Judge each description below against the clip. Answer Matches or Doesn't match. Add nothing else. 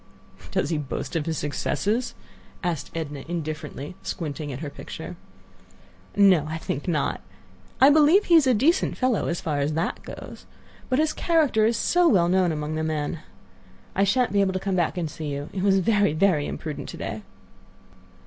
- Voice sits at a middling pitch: Matches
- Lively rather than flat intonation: Matches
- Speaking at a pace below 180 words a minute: Doesn't match